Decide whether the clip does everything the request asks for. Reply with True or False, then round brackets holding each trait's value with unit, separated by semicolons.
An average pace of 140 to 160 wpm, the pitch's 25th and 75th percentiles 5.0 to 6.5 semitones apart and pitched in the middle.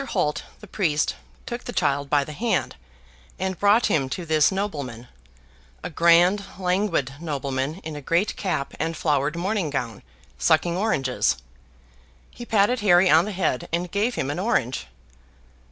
True (155 wpm; 5.6 semitones; 170 Hz)